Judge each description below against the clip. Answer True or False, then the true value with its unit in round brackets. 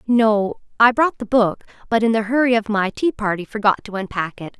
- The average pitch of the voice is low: False (220 Hz)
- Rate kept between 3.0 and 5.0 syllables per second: False (5.3 syllables/s)